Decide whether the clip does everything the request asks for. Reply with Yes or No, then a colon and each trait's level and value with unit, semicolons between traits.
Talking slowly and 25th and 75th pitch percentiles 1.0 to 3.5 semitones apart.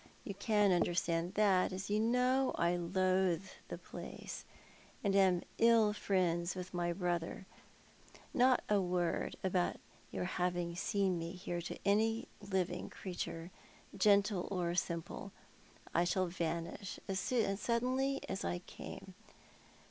Yes: slow, 125 wpm; average, 2.8 semitones